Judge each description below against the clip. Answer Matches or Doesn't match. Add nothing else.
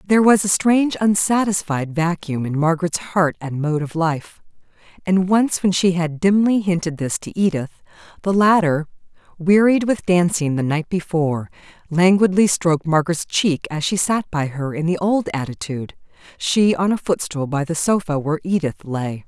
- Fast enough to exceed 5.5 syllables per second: Doesn't match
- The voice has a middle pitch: Matches